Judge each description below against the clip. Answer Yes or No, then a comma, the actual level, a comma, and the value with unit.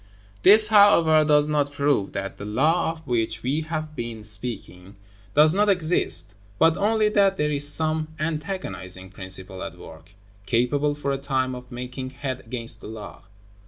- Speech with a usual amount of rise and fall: No, wide, 6.1 semitones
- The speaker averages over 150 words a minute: Yes, average, 160 wpm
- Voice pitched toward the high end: No, medium, 140 Hz